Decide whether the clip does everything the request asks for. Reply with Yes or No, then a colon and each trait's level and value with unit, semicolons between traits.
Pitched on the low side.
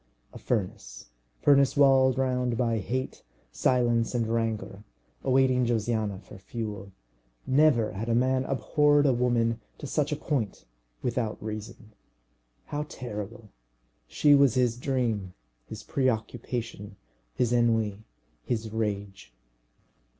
Yes: low, 120 Hz